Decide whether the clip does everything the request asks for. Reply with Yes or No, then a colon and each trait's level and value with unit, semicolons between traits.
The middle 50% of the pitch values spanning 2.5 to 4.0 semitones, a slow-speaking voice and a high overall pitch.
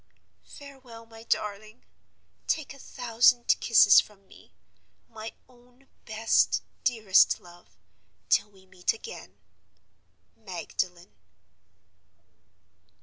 Yes: average, 3.6 semitones; slow, 90 wpm; high, 225 Hz